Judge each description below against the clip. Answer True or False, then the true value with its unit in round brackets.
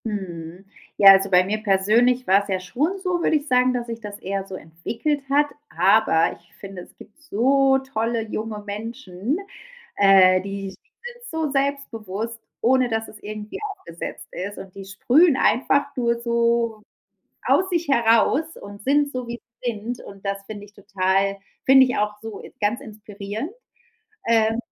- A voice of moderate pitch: False (220 Hz)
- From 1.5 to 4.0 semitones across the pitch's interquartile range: False (4.6 semitones)